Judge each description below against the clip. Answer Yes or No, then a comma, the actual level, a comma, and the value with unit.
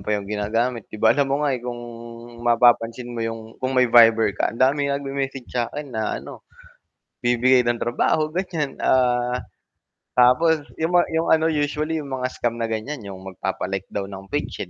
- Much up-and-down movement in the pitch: No, average, 3.7 semitones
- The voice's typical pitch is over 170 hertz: No, low, 125 Hz